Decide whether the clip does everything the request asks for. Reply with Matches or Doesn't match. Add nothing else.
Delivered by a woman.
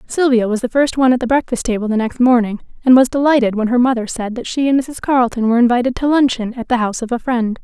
Matches